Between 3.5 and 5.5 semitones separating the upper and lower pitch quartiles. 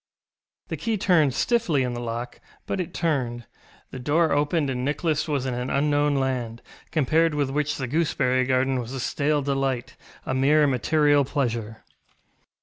No: average, 3.0 semitones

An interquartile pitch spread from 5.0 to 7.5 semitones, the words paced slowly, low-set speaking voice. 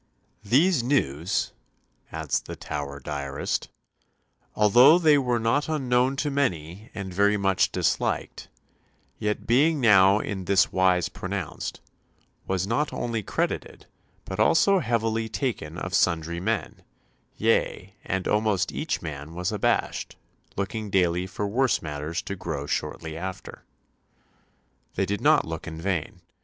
Yes: wide, 5.4 semitones; slow, 130 wpm; low, 100 Hz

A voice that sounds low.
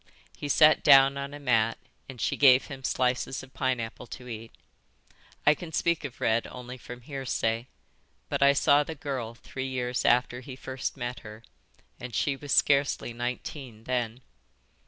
Yes: low, 130 Hz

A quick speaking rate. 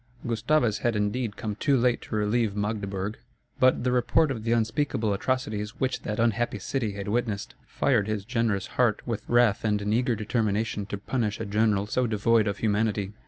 No: average, 180 wpm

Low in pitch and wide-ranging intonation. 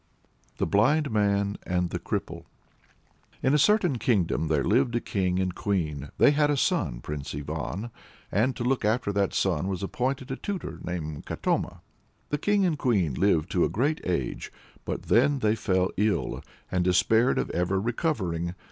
Yes: low, 100 Hz; wide, 6.6 semitones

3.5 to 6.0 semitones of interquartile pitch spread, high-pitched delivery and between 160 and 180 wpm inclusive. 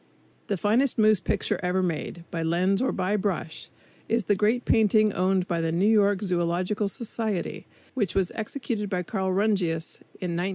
No: average, 3.1 semitones; high, 195 Hz; average, 170 wpm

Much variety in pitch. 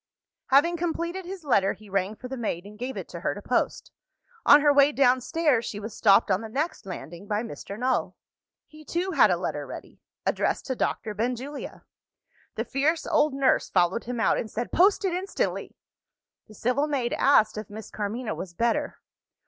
Yes: wide, 5.7 semitones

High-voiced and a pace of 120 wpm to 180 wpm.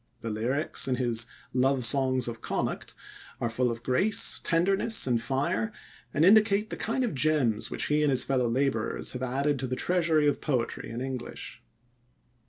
No: low, 130 Hz; average, 175 wpm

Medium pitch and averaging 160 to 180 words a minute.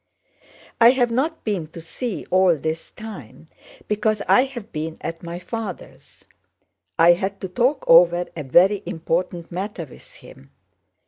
No: medium, 180 Hz; average, 150 wpm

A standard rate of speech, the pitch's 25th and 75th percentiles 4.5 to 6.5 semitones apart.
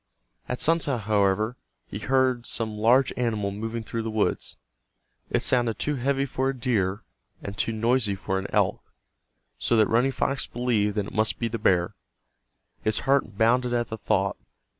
No: average, 165 wpm; average, 3.1 semitones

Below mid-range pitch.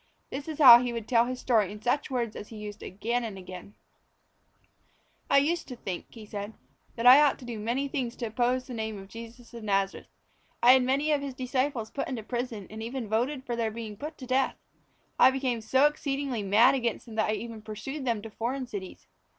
No: high, 240 Hz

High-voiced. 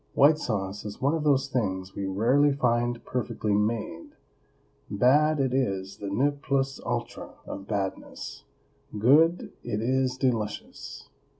No: low, 120 Hz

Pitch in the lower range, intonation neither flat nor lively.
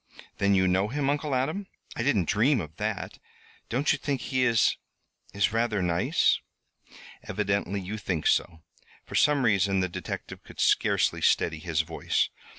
No: low, 100 Hz; wide, 5.9 semitones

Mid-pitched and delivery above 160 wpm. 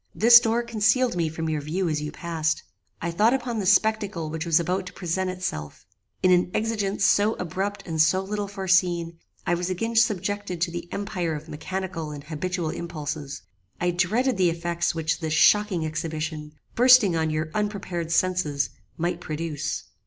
Yes: medium, 175 Hz; average, 170 wpm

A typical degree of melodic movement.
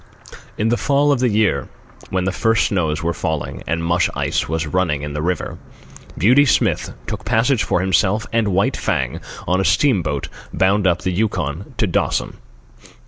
Yes: average, 5.0 semitones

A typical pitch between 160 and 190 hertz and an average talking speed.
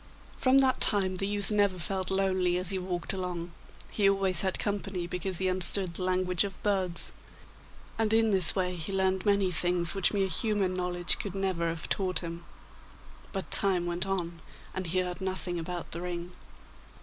Yes: medium, 185 Hz; average, 180 wpm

